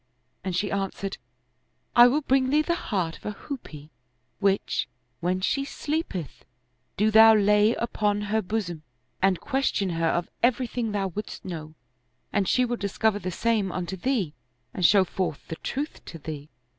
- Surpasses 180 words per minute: No, average, 170 wpm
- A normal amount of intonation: Yes, average, 4.5 semitones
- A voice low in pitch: No, high, 205 Hz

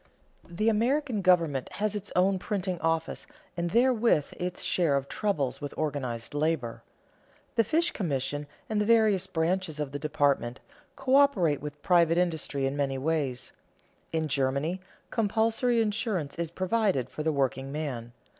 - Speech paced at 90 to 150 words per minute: Yes, average, 140 wpm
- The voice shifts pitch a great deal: Yes, wide, 6.6 semitones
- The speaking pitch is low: No, medium, 165 Hz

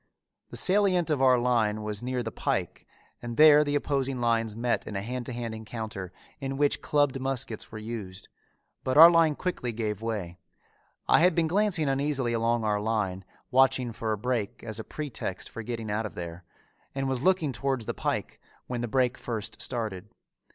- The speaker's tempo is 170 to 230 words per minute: Yes, average, 185 wpm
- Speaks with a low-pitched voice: Yes, low, 120 Hz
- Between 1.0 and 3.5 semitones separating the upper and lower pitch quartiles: No, average, 3.9 semitones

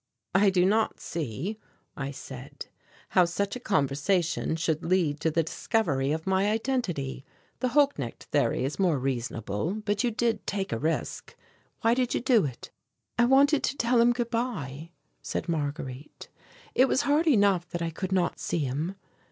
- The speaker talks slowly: No, average, 170 wpm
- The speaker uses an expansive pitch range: Yes, wide, 7.7 semitones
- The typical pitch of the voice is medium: Yes, medium, 180 Hz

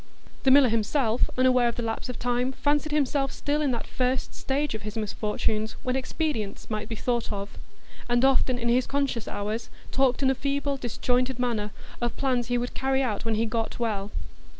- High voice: Yes, high, 245 Hz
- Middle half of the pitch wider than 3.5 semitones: No, average, 2.9 semitones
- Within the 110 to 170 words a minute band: No, average, 195 wpm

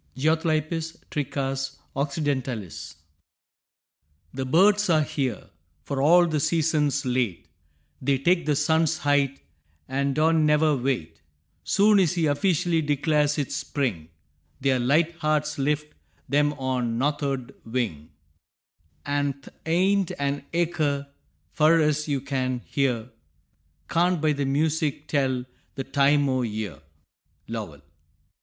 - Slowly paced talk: Yes, slow, 120 wpm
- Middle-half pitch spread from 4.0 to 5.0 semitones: No, average, 3.0 semitones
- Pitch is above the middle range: No, medium, 145 Hz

